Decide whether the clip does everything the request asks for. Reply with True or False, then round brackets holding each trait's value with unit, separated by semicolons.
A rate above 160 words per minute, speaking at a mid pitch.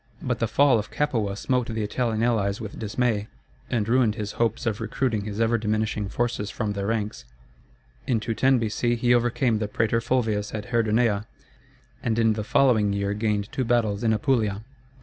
False (175 wpm; 110 Hz)